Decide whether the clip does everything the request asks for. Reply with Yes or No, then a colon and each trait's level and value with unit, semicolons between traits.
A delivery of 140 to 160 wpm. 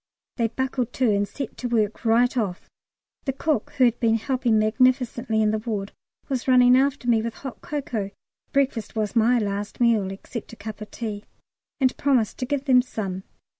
No: average, 185 wpm